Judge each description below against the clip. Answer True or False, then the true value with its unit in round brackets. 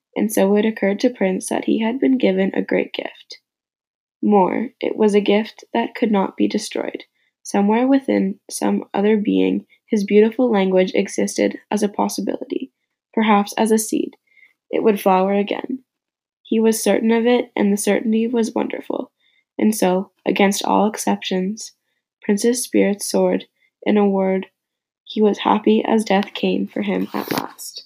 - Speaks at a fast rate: False (160 wpm)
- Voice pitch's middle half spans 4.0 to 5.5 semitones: False (3.2 semitones)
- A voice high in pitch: True (205 Hz)